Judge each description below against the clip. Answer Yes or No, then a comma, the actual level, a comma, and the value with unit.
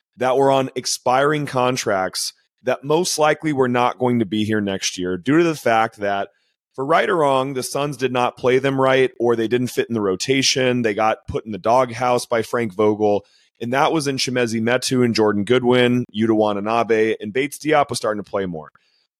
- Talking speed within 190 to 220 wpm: Yes, fast, 205 wpm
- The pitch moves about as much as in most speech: Yes, average, 3.2 semitones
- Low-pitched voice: Yes, low, 125 Hz